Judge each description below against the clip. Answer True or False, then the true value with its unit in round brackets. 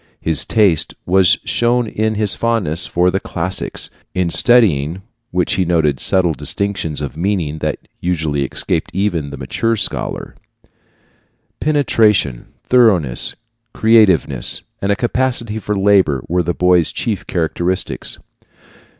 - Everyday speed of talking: False (125 wpm)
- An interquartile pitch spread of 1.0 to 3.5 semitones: False (5.0 semitones)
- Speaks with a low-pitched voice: True (90 Hz)